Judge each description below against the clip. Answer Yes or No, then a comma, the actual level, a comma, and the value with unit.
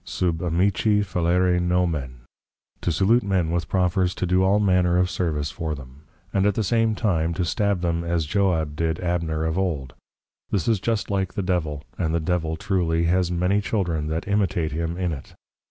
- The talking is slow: No, average, 185 wpm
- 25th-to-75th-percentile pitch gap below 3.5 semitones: Yes, average, 2.8 semitones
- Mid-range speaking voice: No, very low, 90 Hz